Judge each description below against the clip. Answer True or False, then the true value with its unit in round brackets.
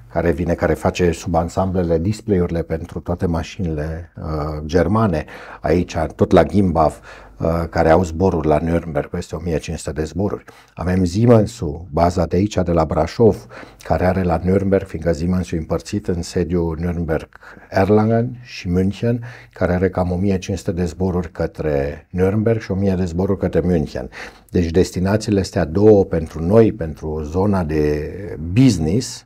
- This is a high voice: False (90 Hz)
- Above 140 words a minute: True (150 wpm)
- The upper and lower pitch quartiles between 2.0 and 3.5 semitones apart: True (2.9 semitones)